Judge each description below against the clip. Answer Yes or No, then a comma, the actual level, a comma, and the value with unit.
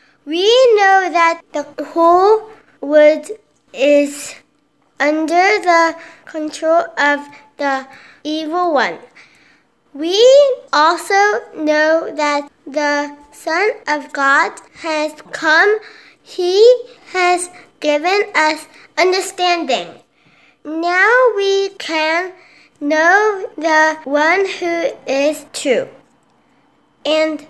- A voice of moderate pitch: No, very high, 330 Hz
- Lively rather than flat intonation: No, average, 4.4 semitones